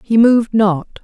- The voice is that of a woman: Yes, female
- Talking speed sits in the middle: Yes, average, 175 wpm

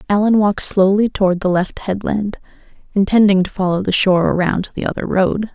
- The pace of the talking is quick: No, average, 185 wpm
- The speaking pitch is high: Yes, high, 195 Hz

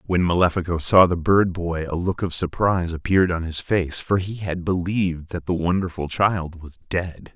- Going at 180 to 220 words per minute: Yes, average, 195 wpm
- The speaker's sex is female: No, male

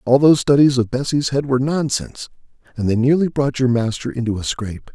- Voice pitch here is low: Yes, low, 130 Hz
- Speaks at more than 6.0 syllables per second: Yes, 6.2 syllables/s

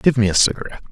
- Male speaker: Yes, male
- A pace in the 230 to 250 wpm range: No, fast, 260 wpm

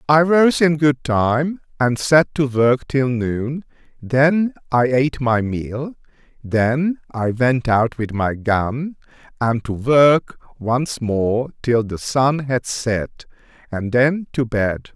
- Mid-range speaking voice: No, low, 130 Hz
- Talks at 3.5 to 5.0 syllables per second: No, 3.1 syllables/s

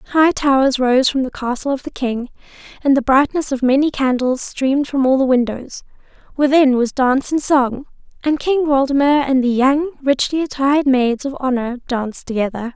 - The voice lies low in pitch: No, very high, 265 Hz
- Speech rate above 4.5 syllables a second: Yes, 5.1 syllables/s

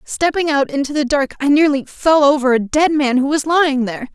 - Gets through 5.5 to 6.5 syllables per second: Yes, 5.6 syllables/s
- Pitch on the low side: No, very high, 285 Hz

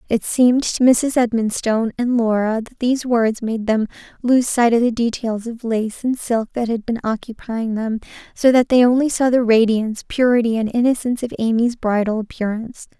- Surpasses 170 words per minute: Yes, average, 185 wpm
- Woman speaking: Yes, female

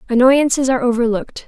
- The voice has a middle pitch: No, very high, 250 Hz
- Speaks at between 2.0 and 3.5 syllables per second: No, 7.0 syllables/s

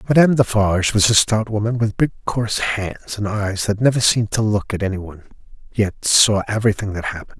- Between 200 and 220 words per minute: Yes, fast, 205 wpm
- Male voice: Yes, male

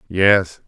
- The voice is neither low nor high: No, very low, 95 Hz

